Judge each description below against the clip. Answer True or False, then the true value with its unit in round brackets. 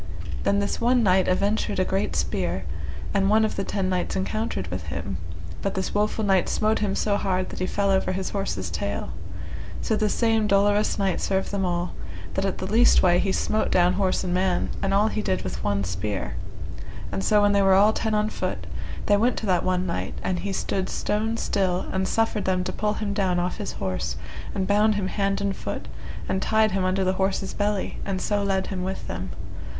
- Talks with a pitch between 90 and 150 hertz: False (195 Hz)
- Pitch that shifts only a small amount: True (2.0 semitones)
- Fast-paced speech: True (215 wpm)